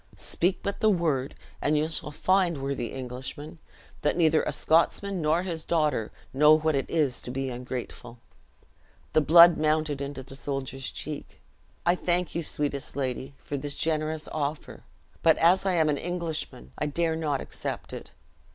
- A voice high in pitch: No, medium, 155 Hz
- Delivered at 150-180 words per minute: Yes, average, 165 wpm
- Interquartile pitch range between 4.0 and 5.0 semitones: No, average, 3.4 semitones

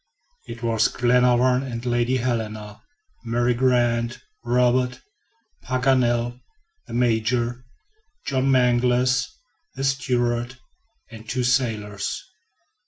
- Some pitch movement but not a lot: No, narrow, 1.3 semitones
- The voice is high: No, low, 120 Hz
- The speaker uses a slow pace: Yes, slow, 95 wpm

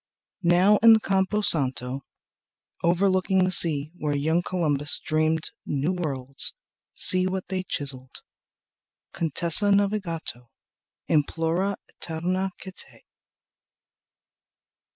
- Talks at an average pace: No, slow, 90 wpm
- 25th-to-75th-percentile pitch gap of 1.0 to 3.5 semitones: No, average, 4.3 semitones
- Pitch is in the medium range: Yes, medium, 170 Hz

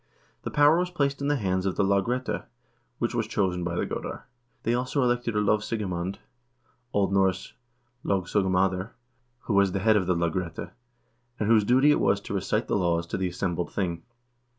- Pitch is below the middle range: Yes, low, 100 Hz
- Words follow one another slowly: No, average, 185 wpm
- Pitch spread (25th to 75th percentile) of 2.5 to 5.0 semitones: Yes, average, 4.2 semitones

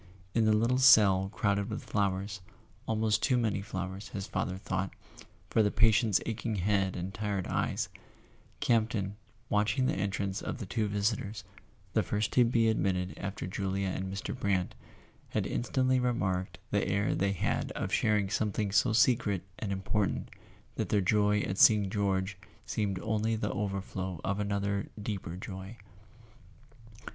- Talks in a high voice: No, low, 100 Hz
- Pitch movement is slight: Yes, narrow, 2.2 semitones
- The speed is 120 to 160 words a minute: Yes, average, 150 wpm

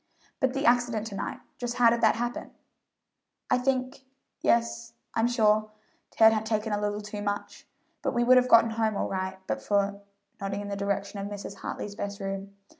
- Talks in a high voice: Yes, high, 215 Hz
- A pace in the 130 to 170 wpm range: No, average, 190 wpm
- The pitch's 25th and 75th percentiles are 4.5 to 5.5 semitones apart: No, average, 2.8 semitones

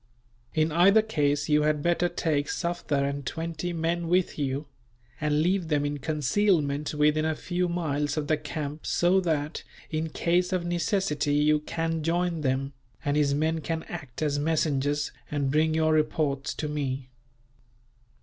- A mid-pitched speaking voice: Yes, medium, 155 Hz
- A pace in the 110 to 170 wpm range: Yes, average, 160 wpm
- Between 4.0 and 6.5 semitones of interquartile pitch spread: No, narrow, 2.6 semitones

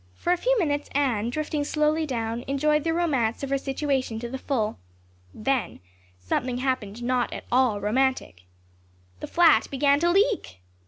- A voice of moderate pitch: No, very high, 270 Hz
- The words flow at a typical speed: Yes, average, 160 wpm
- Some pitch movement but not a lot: Yes, average, 4.1 semitones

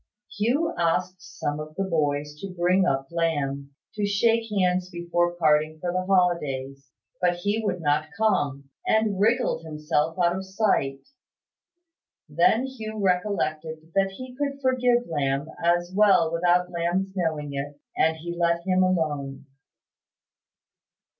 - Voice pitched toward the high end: No, medium, 175 Hz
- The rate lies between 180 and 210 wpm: No, slow, 135 wpm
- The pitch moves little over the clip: No, average, 4.2 semitones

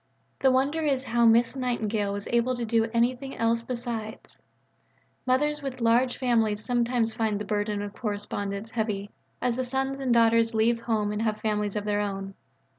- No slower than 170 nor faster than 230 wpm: Yes, average, 175 wpm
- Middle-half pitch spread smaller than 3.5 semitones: Yes, average, 2.8 semitones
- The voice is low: No, high, 230 Hz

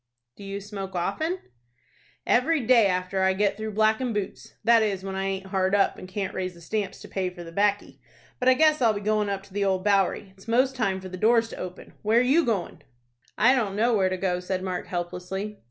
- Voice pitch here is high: Yes, high, 200 Hz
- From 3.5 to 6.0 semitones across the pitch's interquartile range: No, average, 2.8 semitones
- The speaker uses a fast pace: Yes, fast, 230 wpm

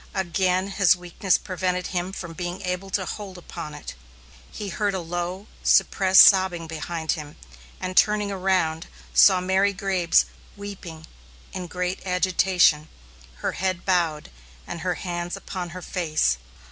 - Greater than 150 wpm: No, average, 145 wpm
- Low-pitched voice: No, medium, 180 Hz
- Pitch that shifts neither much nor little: No, narrow, 1.8 semitones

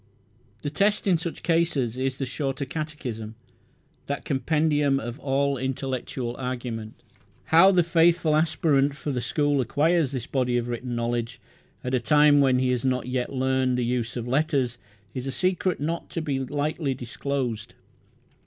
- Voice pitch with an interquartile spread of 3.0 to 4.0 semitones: Yes, average, 3.4 semitones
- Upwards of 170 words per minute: No, average, 160 wpm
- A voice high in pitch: No, low, 135 Hz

